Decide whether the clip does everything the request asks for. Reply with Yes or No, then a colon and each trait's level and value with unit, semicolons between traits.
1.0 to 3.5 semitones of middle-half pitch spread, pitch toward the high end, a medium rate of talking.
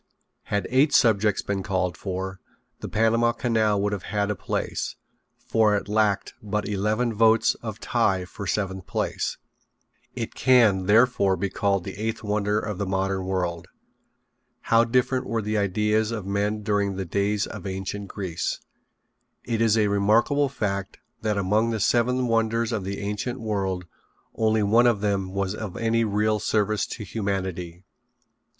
No: narrow, 2.4 semitones; low, 105 Hz; average, 155 wpm